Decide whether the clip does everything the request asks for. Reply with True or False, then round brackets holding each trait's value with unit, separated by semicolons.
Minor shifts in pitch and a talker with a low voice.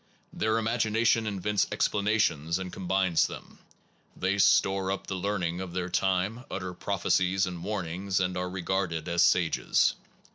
True (2.0 semitones; 95 Hz)